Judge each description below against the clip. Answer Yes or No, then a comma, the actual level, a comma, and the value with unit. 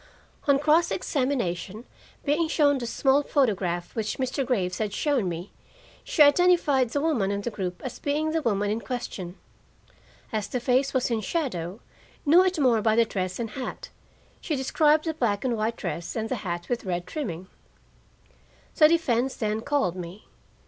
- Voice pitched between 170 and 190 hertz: No, high, 240 Hz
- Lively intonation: Yes, wide, 6.1 semitones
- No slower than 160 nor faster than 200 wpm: Yes, average, 170 wpm